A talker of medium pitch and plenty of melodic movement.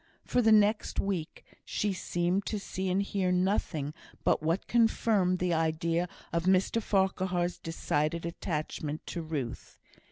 No: medium, 180 Hz; average, 3.2 semitones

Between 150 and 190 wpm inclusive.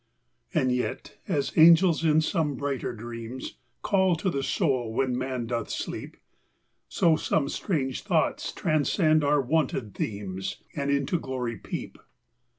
No: slow, 135 wpm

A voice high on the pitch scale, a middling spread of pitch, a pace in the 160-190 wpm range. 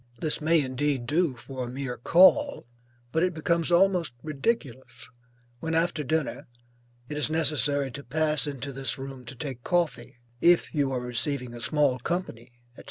No: medium, 145 Hz; average, 4.1 semitones; average, 165 wpm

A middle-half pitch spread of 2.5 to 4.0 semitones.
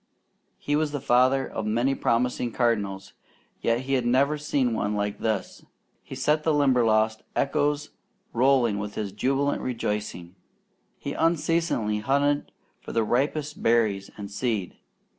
No: average, 4.9 semitones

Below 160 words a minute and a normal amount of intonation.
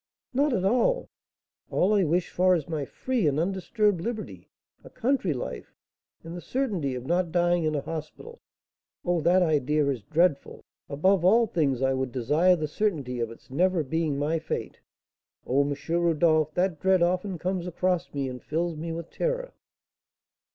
No: average, 170 wpm; average, 3.9 semitones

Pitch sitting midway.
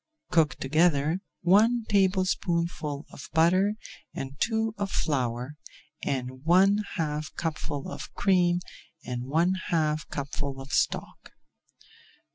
Yes: medium, 165 Hz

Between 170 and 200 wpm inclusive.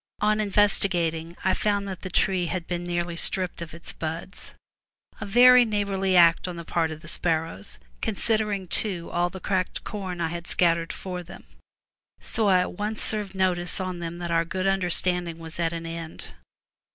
Yes: average, 190 wpm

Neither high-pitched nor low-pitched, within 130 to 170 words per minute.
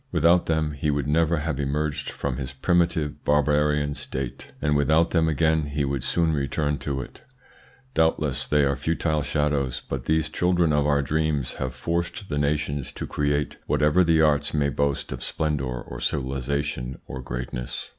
No: very low, 75 Hz; average, 165 wpm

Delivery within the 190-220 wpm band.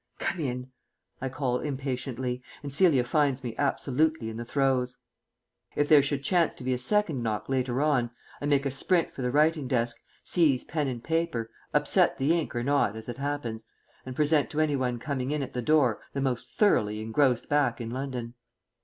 Yes: average, 195 wpm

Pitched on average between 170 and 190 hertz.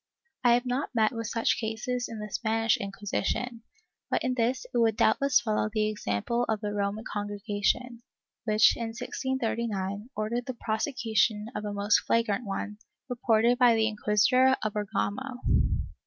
No: high, 225 Hz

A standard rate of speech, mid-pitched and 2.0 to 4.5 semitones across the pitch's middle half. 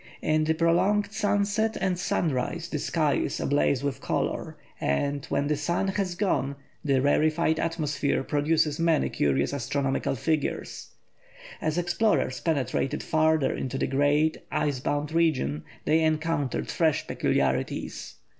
No: slow, 130 wpm; medium, 155 Hz; average, 3.0 semitones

